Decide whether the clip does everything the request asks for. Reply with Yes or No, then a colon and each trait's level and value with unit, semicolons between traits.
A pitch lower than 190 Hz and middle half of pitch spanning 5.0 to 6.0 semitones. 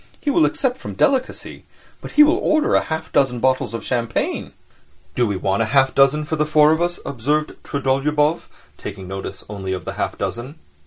Yes: medium, 140 Hz; average, 5.3 semitones